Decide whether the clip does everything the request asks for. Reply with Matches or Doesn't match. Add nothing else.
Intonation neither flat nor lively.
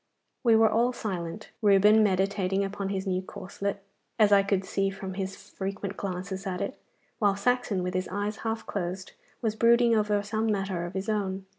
Doesn't match